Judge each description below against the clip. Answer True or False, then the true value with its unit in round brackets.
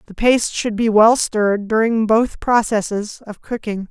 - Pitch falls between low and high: False (220 Hz)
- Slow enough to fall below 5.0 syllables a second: True (4.6 syllables/s)